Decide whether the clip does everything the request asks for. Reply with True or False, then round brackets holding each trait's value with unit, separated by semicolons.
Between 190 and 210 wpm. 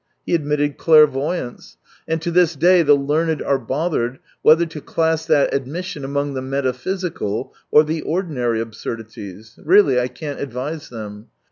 False (150 wpm)